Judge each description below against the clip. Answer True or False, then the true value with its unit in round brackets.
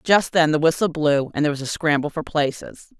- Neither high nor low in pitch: True (155 Hz)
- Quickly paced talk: True (240 wpm)